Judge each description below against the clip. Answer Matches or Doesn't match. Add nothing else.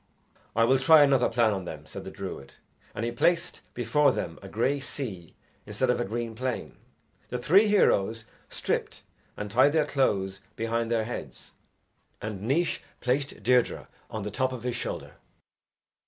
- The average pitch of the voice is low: Matches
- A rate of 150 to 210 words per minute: Matches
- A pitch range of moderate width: Matches